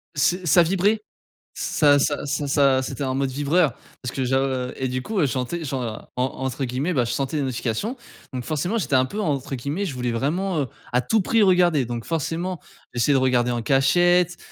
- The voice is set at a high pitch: No, medium, 140 Hz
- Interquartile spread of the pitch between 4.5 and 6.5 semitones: Yes, average, 5.2 semitones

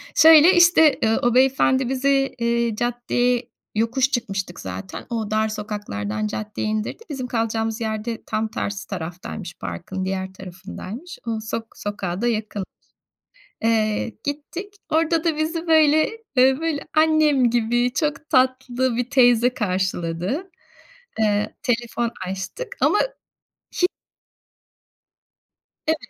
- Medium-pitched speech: No, high, 235 Hz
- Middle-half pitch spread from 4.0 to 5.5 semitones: Yes, average, 4.7 semitones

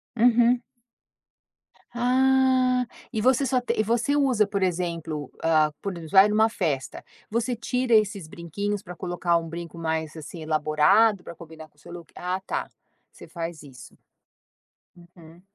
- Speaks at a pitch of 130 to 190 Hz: Yes, medium, 185 Hz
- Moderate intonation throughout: No, wide, 6.3 semitones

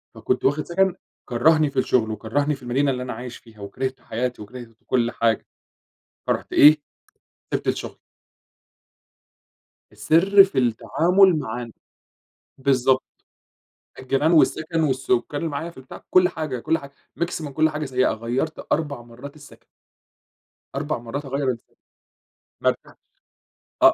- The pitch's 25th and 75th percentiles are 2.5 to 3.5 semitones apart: No, average, 4.1 semitones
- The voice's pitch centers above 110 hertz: Yes, low, 135 Hz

